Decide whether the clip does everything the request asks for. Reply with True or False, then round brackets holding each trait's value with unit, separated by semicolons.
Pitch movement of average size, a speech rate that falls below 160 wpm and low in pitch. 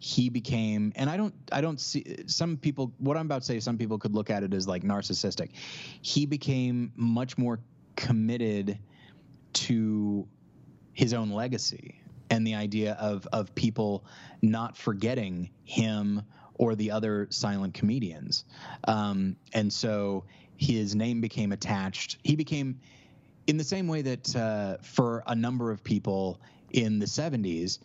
True (4.2 semitones; 150 wpm; 115 Hz)